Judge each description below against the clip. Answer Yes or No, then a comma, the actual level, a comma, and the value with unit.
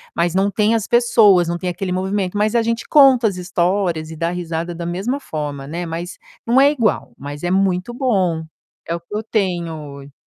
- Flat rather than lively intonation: No, average, 4.1 semitones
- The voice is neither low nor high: Yes, medium, 180 Hz